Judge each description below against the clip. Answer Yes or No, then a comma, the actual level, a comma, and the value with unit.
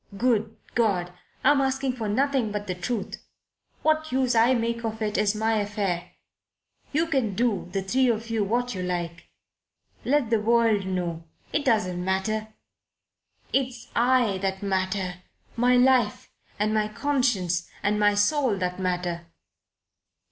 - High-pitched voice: Yes, high, 215 Hz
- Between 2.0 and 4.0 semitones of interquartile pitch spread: No, average, 4.5 semitones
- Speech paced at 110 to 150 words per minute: Yes, average, 145 wpm